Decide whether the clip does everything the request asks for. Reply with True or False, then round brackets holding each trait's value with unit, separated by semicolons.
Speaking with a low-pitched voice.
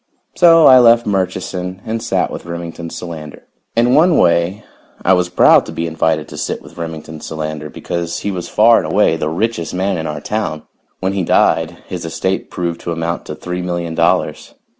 True (85 Hz)